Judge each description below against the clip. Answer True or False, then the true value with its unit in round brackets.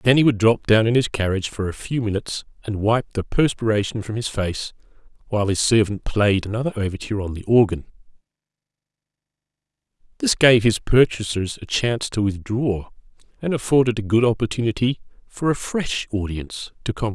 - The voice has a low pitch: True (110 Hz)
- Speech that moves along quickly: False (165 wpm)